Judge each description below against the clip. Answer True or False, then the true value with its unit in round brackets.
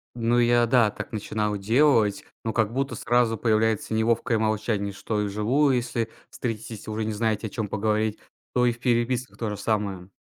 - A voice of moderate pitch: False (110 Hz)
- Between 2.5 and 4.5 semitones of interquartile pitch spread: False (2.1 semitones)